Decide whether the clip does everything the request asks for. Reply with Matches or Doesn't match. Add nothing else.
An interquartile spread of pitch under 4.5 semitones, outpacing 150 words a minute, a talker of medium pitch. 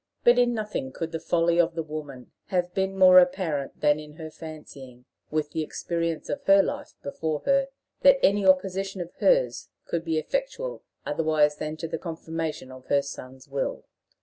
Matches